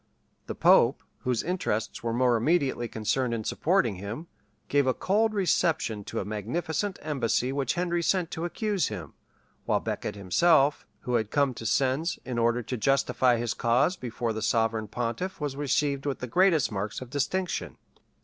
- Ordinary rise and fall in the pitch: No, wide, 6.0 semitones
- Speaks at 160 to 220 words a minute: Yes, average, 170 wpm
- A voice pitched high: No, low, 130 Hz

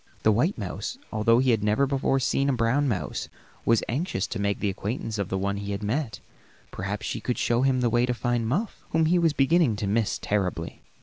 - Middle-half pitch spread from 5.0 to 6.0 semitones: No, average, 4.6 semitones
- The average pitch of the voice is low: Yes, low, 120 Hz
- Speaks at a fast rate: Yes, fast, 225 wpm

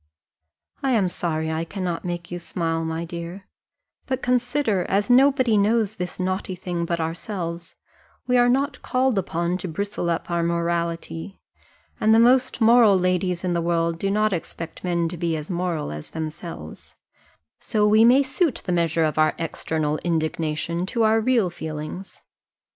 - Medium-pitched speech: Yes, medium, 175 Hz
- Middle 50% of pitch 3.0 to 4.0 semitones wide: No, average, 4.6 semitones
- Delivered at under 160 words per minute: No, average, 165 wpm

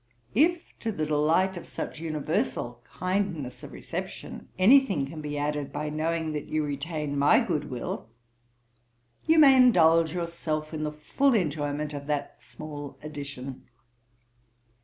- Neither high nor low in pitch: Yes, medium, 155 Hz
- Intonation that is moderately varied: Yes, average, 3.4 semitones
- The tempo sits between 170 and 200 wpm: No, average, 140 wpm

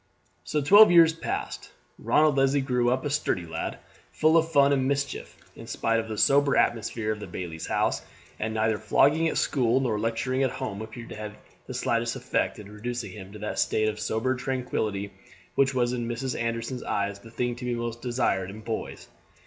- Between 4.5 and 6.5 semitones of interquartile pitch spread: No, average, 3.7 semitones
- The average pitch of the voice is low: Yes, low, 120 Hz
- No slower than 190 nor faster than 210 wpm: Yes, average, 195 wpm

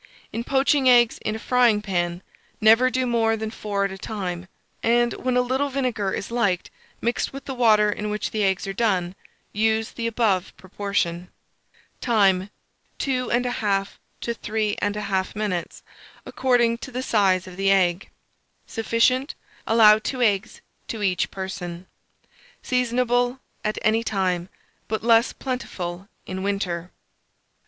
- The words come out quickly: No, average, 145 wpm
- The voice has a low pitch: No, high, 215 Hz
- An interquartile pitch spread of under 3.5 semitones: No, average, 3.8 semitones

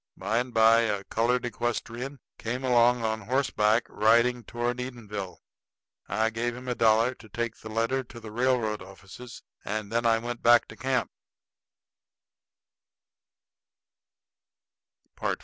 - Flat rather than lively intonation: Yes, narrow, 1.9 semitones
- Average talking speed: No, slow, 130 wpm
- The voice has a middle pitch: No, low, 115 Hz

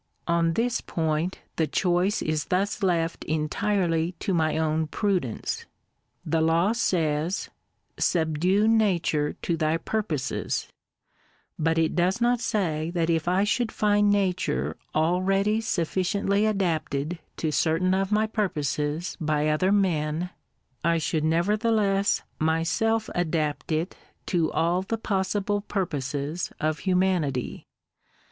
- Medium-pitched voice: Yes, medium, 175 Hz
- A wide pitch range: No, average, 4.0 semitones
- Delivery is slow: Yes, slow, 125 wpm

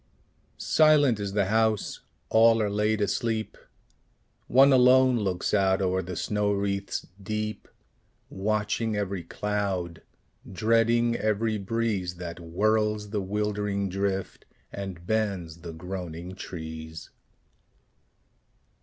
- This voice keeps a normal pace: No, slow, 105 wpm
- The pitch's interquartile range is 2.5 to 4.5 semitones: Yes, average, 2.8 semitones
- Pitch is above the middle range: No, low, 100 Hz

